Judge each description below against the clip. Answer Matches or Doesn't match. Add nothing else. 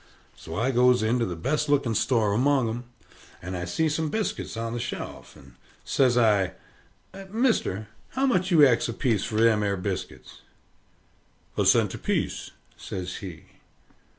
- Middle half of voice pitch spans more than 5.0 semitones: Matches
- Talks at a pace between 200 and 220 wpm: Doesn't match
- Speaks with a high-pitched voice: Doesn't match